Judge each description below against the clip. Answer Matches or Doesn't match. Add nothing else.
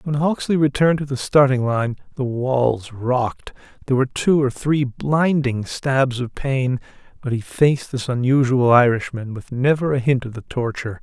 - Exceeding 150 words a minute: Matches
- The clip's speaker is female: Doesn't match